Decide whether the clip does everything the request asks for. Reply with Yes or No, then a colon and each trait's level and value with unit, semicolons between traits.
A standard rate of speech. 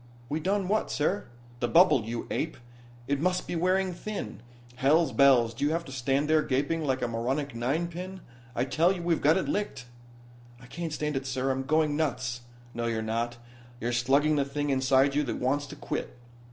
Yes: average, 195 wpm